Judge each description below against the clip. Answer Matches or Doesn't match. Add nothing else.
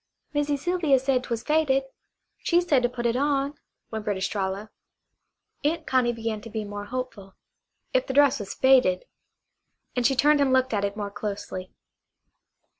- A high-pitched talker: Matches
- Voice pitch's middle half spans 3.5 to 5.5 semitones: Matches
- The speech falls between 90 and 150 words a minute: Doesn't match